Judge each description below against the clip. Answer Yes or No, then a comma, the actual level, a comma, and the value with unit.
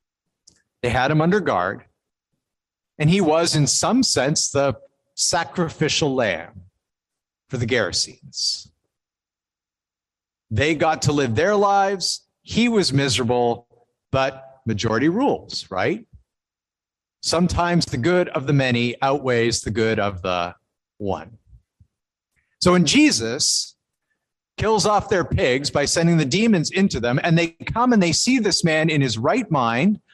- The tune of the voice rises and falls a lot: Yes, wide, 6.5 semitones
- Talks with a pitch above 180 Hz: No, medium, 145 Hz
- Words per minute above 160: No, slow, 135 wpm